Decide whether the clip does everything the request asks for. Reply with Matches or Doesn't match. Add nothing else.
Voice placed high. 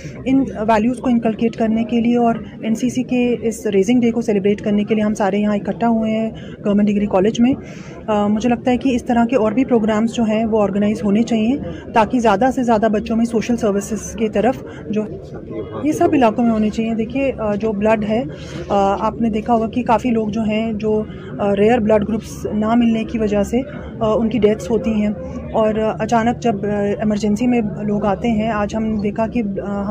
Matches